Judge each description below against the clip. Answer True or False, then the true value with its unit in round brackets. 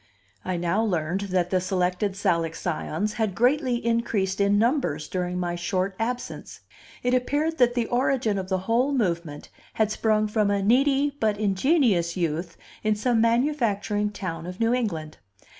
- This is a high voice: True (205 Hz)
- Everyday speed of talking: True (160 wpm)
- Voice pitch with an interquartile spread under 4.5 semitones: False (4.9 semitones)